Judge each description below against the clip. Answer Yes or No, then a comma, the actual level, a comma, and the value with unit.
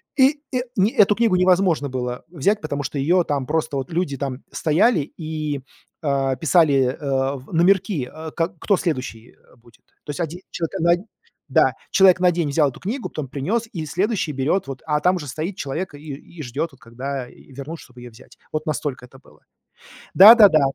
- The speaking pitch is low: No, medium, 155 Hz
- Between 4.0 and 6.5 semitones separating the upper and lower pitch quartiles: Yes, average, 4.9 semitones